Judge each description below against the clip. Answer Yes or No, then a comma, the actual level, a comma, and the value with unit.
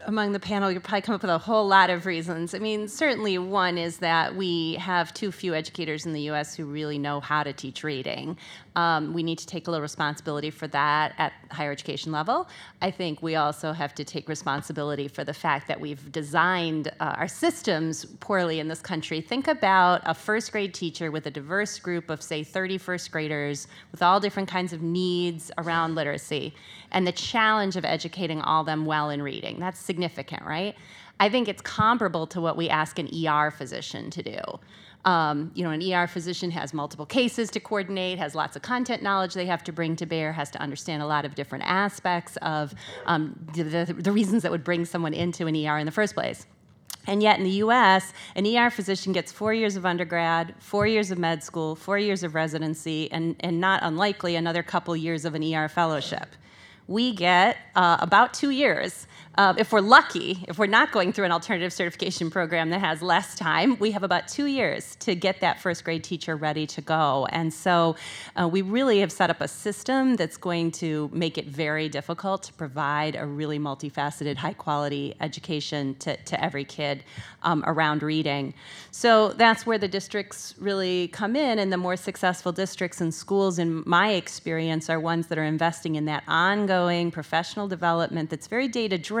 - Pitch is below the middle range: No, medium, 170 Hz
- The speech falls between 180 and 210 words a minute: Yes, average, 200 wpm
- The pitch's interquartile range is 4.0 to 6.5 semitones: No, average, 3.6 semitones